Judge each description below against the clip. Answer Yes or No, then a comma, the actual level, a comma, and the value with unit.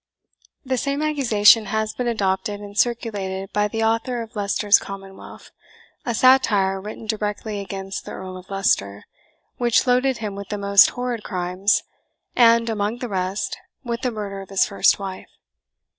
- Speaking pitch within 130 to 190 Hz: No, high, 210 Hz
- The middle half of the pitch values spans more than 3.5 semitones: No, average, 3.1 semitones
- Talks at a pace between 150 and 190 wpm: Yes, average, 160 wpm